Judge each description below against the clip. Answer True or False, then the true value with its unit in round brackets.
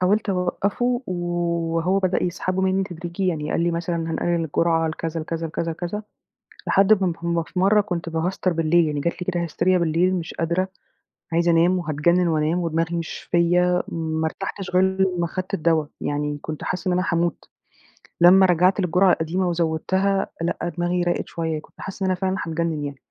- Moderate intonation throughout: False (2.1 semitones)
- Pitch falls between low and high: True (175 Hz)